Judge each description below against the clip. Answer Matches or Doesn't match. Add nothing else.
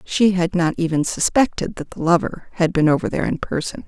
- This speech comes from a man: Doesn't match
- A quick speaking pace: Matches